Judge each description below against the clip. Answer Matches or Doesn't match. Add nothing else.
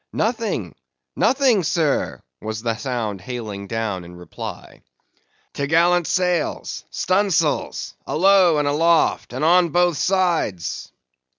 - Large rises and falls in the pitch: Matches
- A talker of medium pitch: Matches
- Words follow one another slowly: Matches